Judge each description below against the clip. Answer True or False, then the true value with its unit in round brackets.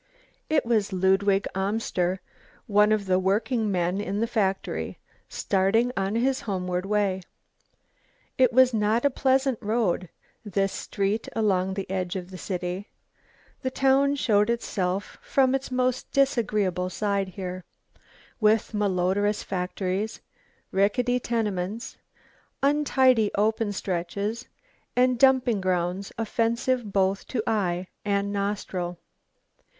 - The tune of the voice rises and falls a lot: False (3.7 semitones)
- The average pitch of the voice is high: True (205 Hz)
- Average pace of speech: False (115 wpm)